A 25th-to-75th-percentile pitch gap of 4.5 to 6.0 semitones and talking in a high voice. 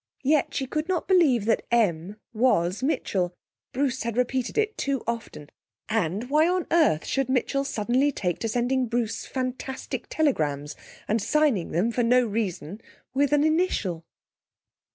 Yes: average, 5.2 semitones; high, 245 Hz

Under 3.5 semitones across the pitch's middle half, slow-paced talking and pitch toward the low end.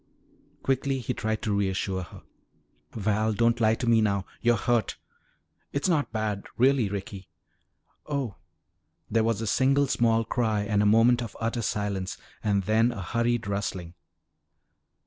No: average, 2.8 semitones; average, 150 wpm; low, 110 Hz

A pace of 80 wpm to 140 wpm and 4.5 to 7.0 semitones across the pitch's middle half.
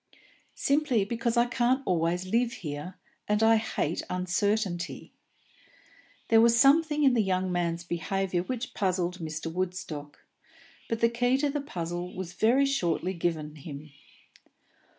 Yes: slow, 135 wpm; wide, 5.5 semitones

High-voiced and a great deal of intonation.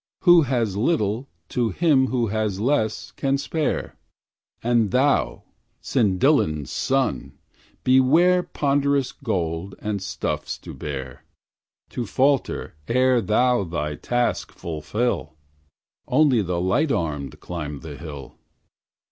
No: low, 115 Hz; wide, 7.8 semitones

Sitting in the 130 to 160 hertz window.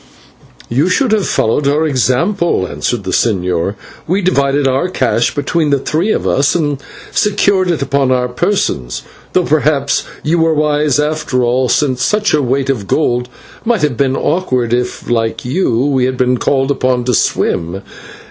Yes: medium, 140 Hz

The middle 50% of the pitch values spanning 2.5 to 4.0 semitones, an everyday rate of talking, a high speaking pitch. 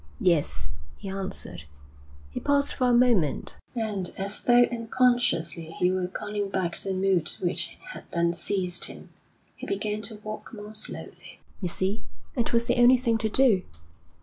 No: average, 4.6 semitones; average, 160 wpm; high, 200 Hz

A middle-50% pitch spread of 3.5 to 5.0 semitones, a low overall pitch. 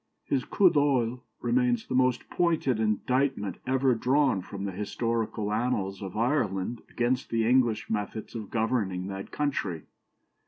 Yes: average, 4.1 semitones; low, 115 Hz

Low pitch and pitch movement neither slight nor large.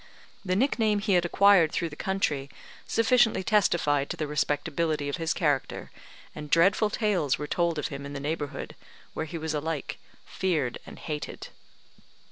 No: medium, 160 Hz; average, 4.6 semitones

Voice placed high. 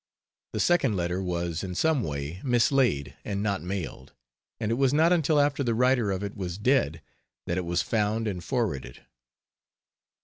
No: low, 105 Hz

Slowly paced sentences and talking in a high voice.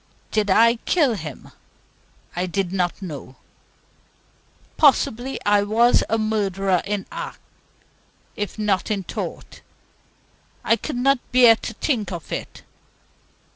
Yes: slow, 120 wpm; high, 210 Hz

